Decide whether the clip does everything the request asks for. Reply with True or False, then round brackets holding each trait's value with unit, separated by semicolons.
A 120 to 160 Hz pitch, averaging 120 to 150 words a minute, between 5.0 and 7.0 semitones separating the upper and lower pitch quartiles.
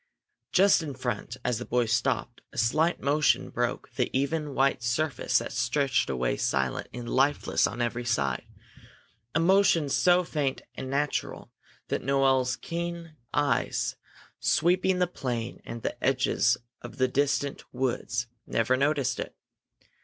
False (135 Hz; 140 wpm; 4.2 semitones)